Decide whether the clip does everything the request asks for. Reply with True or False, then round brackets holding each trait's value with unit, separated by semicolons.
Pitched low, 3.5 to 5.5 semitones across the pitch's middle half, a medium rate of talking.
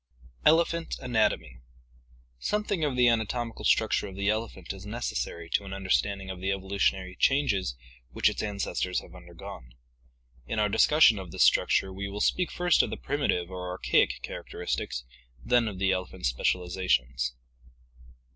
True (100 Hz; 4.3 semitones; 150 wpm)